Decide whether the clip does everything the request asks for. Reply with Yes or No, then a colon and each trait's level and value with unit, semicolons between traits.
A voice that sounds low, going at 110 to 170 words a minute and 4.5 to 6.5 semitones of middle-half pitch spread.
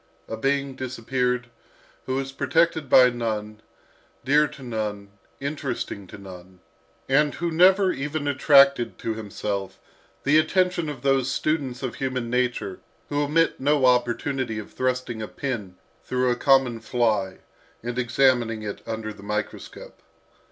No: low, 125 Hz; slow, 135 wpm; average, 4.0 semitones